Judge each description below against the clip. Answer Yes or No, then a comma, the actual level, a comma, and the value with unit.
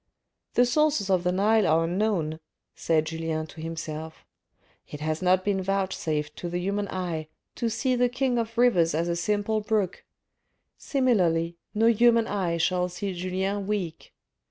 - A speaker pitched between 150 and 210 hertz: Yes, medium, 185 Hz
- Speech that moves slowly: No, average, 160 wpm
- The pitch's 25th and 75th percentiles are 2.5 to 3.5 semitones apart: No, average, 4.7 semitones